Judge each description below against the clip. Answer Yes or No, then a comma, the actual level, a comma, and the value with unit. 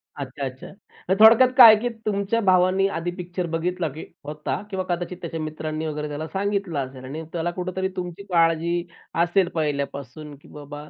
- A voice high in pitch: No, medium, 170 Hz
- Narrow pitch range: No, average, 3.7 semitones